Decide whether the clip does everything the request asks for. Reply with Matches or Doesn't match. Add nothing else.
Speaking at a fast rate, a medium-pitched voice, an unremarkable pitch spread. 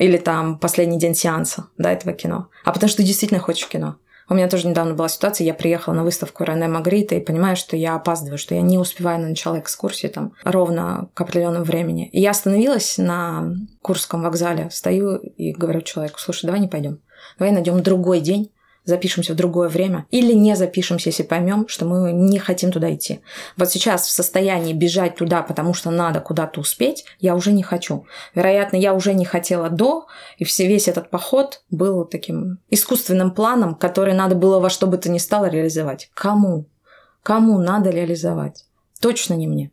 Doesn't match